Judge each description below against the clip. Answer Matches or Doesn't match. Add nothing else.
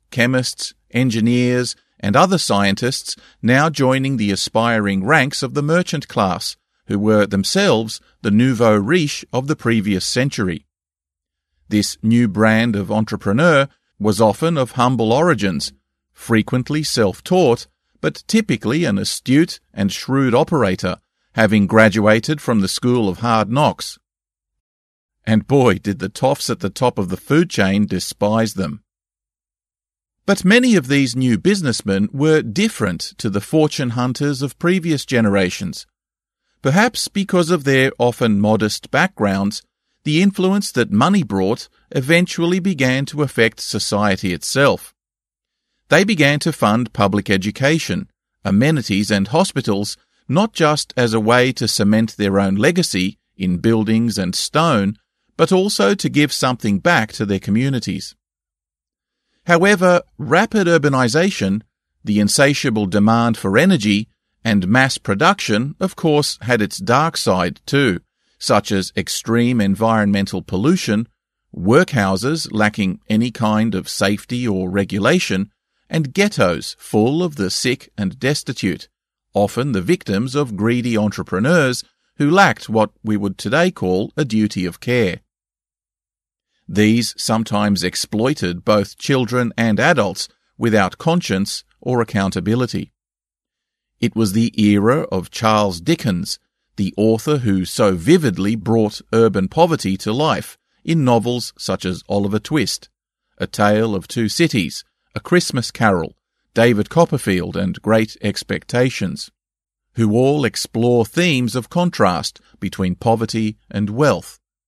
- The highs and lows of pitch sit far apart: Matches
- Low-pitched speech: Matches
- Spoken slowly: Matches